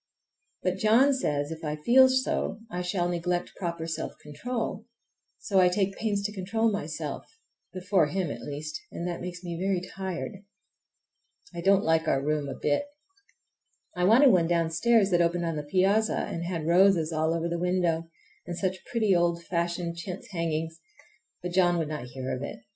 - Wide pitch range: No, average, 3.0 semitones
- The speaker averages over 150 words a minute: Yes, average, 170 wpm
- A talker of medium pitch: Yes, medium, 175 Hz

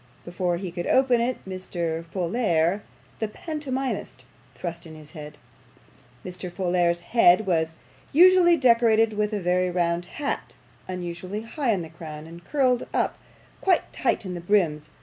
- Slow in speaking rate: No, average, 150 wpm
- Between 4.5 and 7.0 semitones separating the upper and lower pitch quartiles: Yes, average, 5.3 semitones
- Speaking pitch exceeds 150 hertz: Yes, medium, 185 Hz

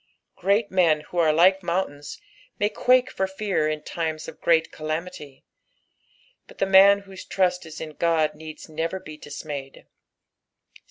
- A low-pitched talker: No, medium, 170 Hz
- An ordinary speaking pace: Yes, average, 150 wpm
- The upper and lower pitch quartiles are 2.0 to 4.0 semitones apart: Yes, average, 3.6 semitones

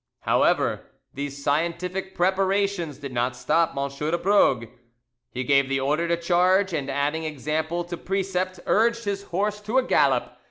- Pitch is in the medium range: Yes, medium, 170 Hz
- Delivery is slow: No, average, 155 wpm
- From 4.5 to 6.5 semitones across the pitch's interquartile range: Yes, average, 5.2 semitones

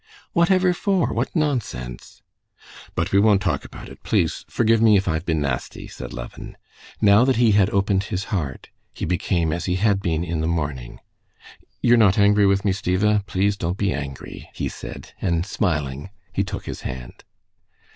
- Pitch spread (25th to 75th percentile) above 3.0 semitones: Yes, average, 4.3 semitones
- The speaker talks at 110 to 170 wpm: No, average, 180 wpm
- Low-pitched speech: Yes, very low, 95 Hz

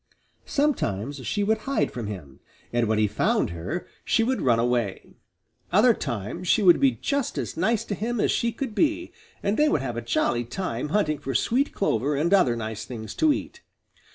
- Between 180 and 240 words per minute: Yes, average, 195 wpm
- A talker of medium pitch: Yes, medium, 155 Hz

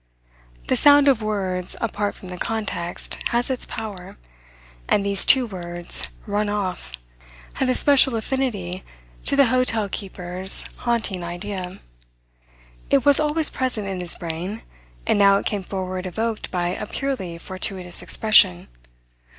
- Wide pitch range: No, average, 4.5 semitones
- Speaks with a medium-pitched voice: No, high, 200 Hz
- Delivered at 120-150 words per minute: Yes, average, 140 wpm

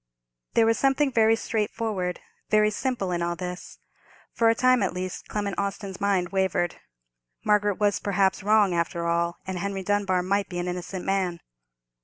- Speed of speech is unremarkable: Yes, average, 165 wpm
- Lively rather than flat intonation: No, average, 2.8 semitones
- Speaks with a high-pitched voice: Yes, high, 195 Hz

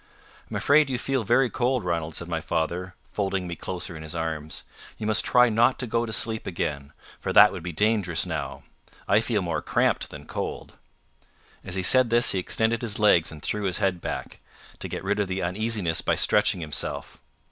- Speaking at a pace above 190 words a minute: Yes, average, 200 wpm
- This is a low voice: Yes, low, 100 Hz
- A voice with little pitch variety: No, average, 4.7 semitones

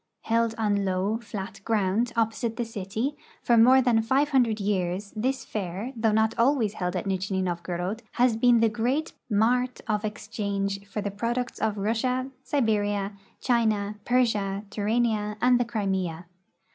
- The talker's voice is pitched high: Yes, high, 220 Hz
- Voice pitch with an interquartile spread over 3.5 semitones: No, average, 3.0 semitones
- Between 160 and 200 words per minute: No, average, 150 wpm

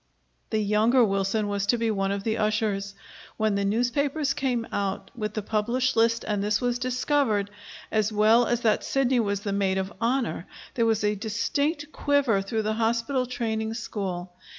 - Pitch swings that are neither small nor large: Yes, average, 3.1 semitones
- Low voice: No, high, 220 Hz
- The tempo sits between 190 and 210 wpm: No, average, 175 wpm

